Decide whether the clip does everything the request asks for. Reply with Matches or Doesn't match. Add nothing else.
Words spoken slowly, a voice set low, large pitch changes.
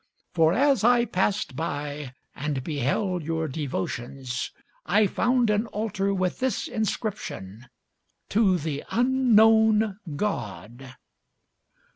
Doesn't match